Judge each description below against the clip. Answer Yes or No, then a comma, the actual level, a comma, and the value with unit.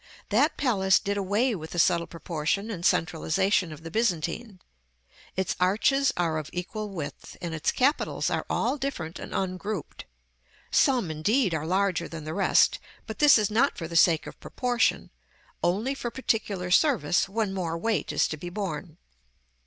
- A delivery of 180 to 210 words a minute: No, average, 165 wpm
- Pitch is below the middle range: No, high, 190 Hz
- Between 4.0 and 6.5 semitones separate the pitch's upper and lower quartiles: Yes, average, 4.9 semitones